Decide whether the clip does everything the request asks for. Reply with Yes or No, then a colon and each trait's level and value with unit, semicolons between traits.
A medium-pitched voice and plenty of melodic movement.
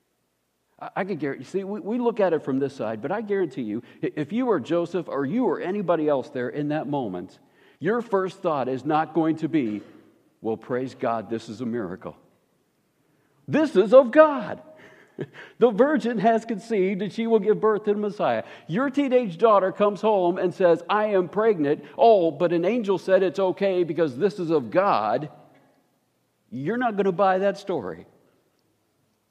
Yes: medium, 180 Hz; wide, 6.8 semitones